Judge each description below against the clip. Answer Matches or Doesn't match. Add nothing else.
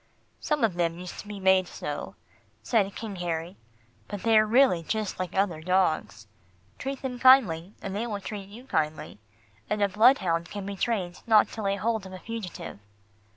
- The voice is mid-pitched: Doesn't match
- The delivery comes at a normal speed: Matches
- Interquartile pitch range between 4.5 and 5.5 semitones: Doesn't match